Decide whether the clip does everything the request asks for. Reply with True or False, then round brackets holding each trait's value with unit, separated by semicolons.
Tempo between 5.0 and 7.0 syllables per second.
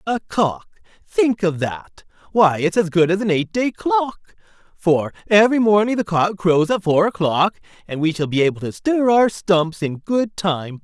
False (4.4 syllables/s)